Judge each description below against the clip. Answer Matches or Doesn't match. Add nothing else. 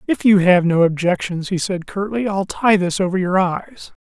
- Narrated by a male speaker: Matches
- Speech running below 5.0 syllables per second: Matches